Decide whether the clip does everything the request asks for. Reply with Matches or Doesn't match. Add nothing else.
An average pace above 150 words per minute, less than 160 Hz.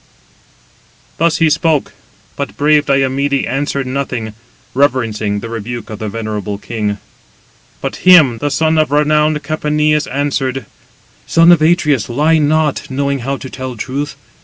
Doesn't match